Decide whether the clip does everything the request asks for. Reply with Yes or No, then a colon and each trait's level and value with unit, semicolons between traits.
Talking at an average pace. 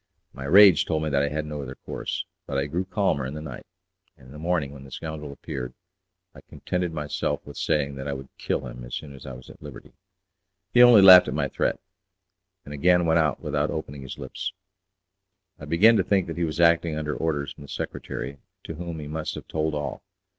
No: fast, 225 wpm